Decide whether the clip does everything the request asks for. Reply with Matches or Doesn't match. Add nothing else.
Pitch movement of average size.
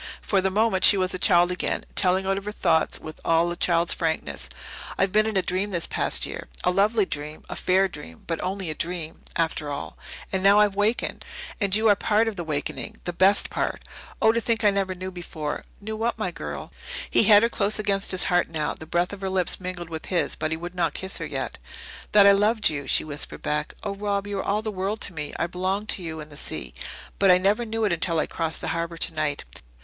Matches